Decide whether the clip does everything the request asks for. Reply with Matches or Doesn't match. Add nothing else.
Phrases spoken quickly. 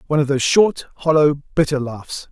Doesn't match